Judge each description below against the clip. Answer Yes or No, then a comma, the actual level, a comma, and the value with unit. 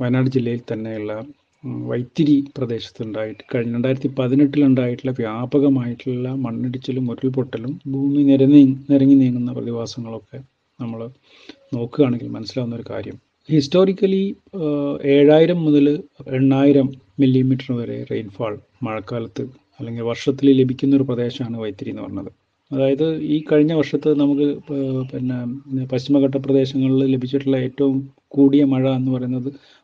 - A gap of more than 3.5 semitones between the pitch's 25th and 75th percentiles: No, narrow, 2.4 semitones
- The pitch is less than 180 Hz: Yes, low, 135 Hz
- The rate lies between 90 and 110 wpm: Yes, average, 105 wpm